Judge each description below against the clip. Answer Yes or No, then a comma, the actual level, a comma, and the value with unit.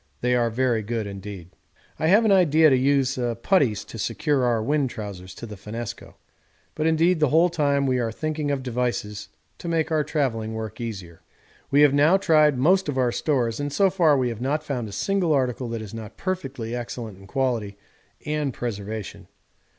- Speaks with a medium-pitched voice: No, low, 130 Hz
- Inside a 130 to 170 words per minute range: No, average, 190 wpm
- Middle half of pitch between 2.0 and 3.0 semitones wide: No, average, 5.3 semitones